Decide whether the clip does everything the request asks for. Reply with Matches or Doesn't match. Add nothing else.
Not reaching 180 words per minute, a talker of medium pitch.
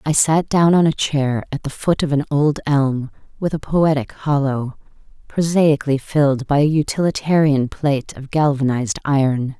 Matches